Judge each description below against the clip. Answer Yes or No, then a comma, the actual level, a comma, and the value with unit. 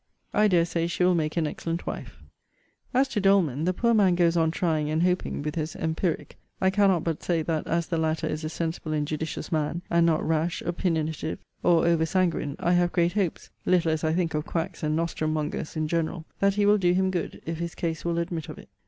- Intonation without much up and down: Yes, narrow, 2.1 semitones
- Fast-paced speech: Yes, fast, 230 wpm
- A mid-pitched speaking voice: Yes, medium, 170 Hz